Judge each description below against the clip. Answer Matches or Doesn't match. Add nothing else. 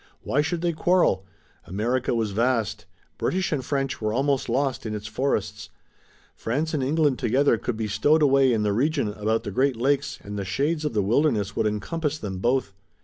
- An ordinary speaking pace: Matches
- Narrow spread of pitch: Doesn't match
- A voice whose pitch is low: Matches